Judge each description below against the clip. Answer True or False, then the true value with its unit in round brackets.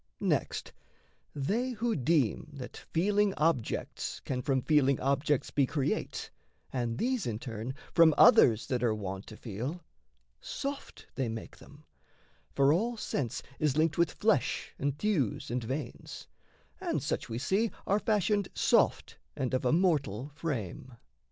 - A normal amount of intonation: False (5.8 semitones)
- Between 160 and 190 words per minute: False (145 wpm)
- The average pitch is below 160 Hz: True (140 Hz)